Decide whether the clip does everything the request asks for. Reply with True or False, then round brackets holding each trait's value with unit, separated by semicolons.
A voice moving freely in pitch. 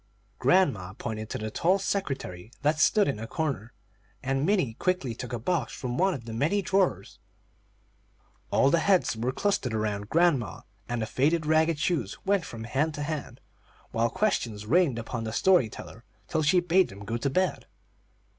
True (7.6 semitones)